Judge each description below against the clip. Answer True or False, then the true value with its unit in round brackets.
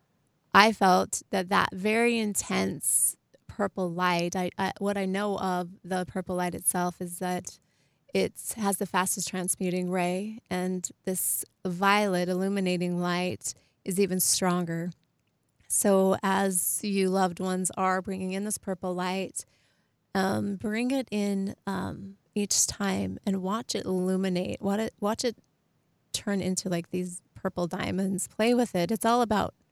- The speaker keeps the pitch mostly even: True (1.7 semitones)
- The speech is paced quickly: False (140 wpm)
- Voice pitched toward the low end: False (190 Hz)